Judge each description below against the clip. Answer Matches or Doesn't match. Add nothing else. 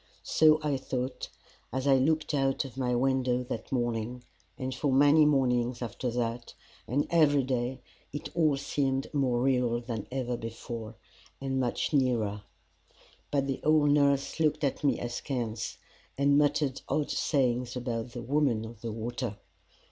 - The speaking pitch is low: Matches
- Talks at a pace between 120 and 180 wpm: Matches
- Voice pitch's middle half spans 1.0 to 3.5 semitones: Matches